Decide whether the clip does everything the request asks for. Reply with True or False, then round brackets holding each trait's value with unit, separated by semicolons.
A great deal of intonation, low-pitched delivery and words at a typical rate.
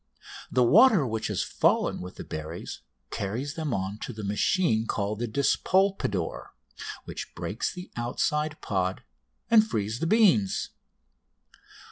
False (7.8 semitones; 115 Hz; 130 wpm)